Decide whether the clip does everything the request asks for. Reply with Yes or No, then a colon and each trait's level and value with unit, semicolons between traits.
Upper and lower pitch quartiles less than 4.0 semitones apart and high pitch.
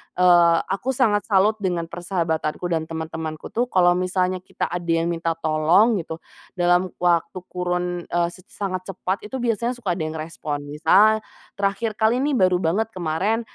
No: average, 3.5 semitones; medium, 180 Hz